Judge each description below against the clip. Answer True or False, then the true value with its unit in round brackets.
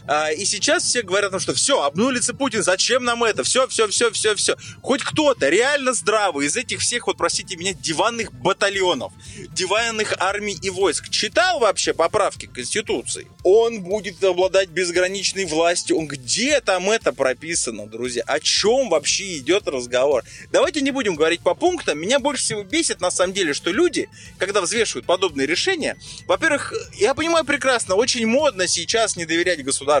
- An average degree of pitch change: False (6.7 semitones)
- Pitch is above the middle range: True (200 Hz)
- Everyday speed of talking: False (165 wpm)